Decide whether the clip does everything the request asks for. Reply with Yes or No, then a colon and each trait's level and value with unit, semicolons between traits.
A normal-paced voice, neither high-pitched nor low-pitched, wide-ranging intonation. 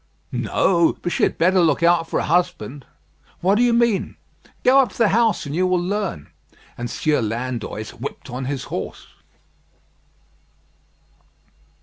Yes: average, 150 wpm; medium, 175 Hz; wide, 6.4 semitones